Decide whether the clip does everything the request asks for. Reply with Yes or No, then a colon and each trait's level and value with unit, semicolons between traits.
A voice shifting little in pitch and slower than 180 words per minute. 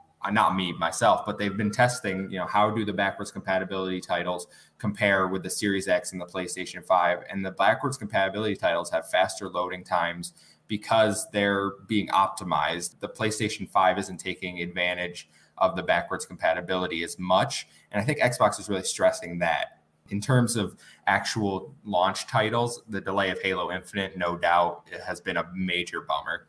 Yes: narrow, 2.3 semitones; average, 170 wpm